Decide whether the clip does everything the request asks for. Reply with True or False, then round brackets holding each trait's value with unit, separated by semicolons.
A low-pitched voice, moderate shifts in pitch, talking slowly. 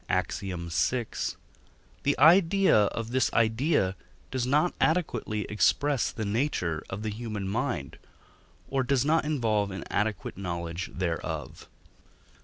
False (110 Hz; 6.3 semitones; 120 wpm)